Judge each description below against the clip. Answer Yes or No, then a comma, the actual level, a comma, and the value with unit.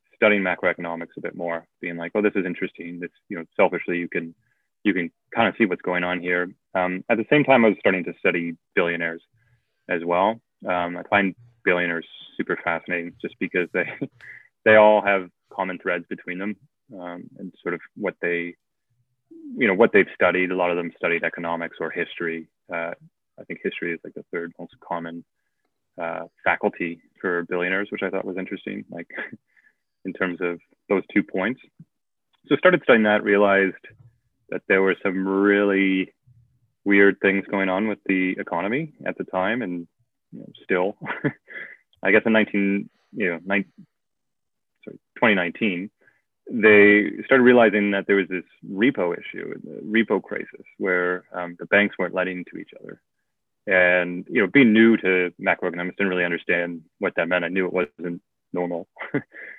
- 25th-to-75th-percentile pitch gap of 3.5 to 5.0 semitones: No, average, 3.0 semitones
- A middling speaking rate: Yes, average, 175 wpm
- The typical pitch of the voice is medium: No, very low, 95 Hz